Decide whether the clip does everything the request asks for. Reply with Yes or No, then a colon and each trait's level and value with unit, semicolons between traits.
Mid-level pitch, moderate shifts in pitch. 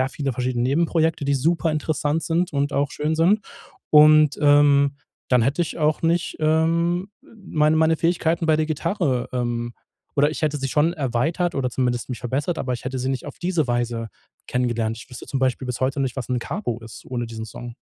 Yes: medium, 145 Hz; average, 4.3 semitones